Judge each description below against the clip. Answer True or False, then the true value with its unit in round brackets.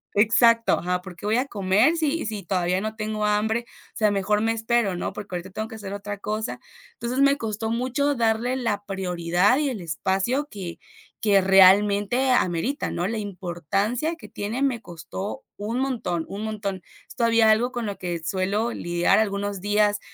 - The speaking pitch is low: False (210 Hz)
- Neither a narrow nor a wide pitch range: True (3.3 semitones)